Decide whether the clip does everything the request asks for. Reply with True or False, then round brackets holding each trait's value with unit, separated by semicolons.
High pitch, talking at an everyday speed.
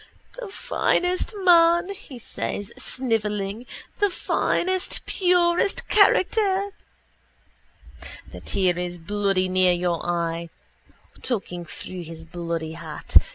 False (205 Hz; 100 wpm)